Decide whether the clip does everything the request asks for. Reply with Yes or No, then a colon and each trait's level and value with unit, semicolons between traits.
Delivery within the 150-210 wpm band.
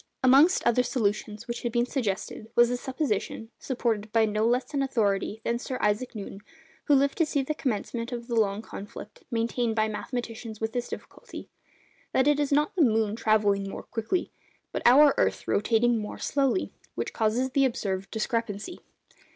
Yes: average, 175 wpm